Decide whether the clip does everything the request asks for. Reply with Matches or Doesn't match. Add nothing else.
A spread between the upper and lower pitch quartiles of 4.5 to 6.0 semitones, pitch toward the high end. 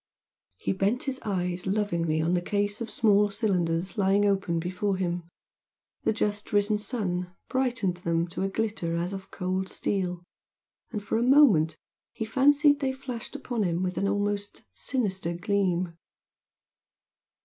Doesn't match